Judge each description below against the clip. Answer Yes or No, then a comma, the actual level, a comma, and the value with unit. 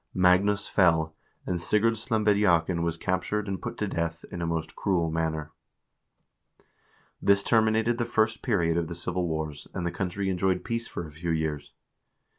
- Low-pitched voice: Yes, very low, 90 Hz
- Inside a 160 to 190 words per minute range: Yes, average, 165 wpm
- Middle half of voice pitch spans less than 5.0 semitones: Yes, average, 4.0 semitones